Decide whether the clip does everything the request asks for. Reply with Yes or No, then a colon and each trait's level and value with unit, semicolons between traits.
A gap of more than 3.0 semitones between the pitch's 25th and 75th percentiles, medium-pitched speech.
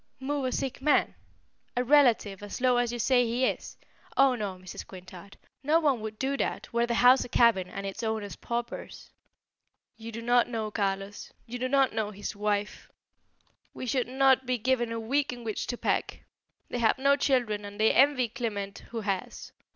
No: average, 3.6 semitones; high, 235 Hz